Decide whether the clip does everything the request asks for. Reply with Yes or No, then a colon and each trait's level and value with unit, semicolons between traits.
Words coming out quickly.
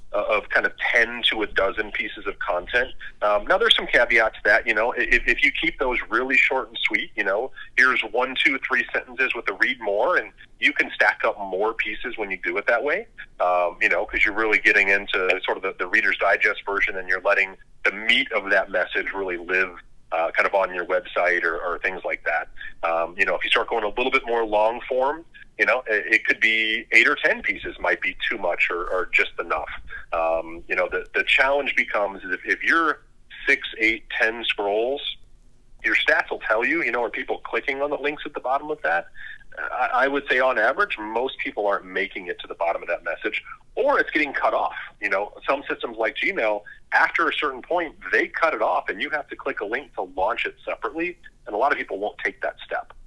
Yes: fast, 235 wpm